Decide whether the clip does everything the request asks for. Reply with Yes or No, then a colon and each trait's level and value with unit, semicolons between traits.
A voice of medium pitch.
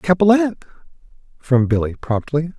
Yes: medium, 155 Hz